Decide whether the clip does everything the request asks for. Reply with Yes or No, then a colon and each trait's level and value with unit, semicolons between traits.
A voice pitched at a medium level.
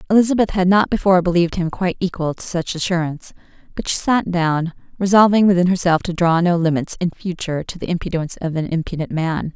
Yes: medium, 175 Hz